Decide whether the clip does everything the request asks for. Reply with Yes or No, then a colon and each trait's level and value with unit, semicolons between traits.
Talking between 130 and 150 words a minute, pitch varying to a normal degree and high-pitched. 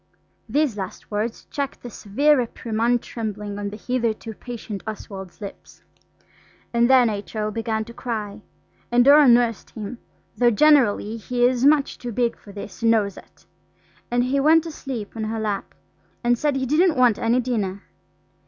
No: average, 165 wpm; average, 3.1 semitones; high, 235 Hz